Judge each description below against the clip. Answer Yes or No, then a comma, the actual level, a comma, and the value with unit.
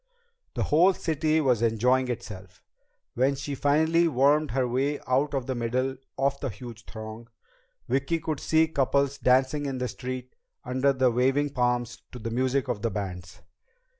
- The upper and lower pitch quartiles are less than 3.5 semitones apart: Yes, narrow, 2.6 semitones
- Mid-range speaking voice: No, low, 130 Hz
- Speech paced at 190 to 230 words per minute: No, average, 165 wpm